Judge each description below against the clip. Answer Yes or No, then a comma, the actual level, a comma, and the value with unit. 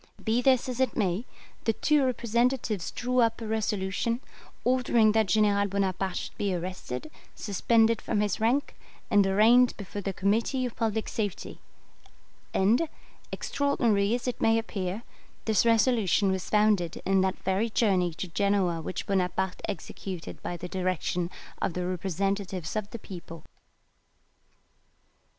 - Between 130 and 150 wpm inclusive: Yes, average, 140 wpm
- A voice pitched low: No, high, 205 Hz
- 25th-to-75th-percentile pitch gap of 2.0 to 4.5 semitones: Yes, average, 3.4 semitones